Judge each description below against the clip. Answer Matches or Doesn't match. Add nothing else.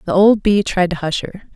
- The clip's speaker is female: Matches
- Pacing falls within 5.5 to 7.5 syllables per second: Doesn't match